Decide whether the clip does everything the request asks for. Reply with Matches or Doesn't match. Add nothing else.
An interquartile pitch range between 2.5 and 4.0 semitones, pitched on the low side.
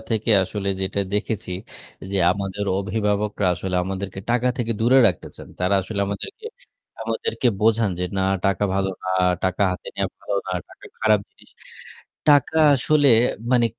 Matches